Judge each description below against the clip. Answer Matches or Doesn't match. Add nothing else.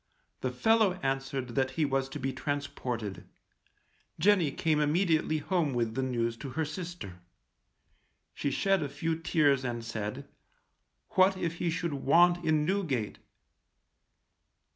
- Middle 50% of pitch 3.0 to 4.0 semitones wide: Doesn't match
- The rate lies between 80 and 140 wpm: Matches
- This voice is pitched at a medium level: Matches